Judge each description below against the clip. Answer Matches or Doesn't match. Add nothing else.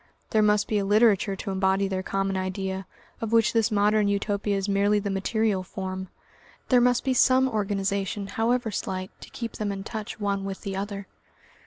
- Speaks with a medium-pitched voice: Doesn't match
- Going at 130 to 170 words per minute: Doesn't match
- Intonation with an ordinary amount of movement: Doesn't match